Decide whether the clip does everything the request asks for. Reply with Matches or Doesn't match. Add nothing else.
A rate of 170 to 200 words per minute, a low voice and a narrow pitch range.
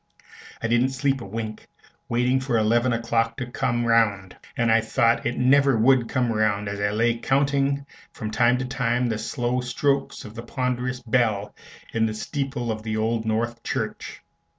Matches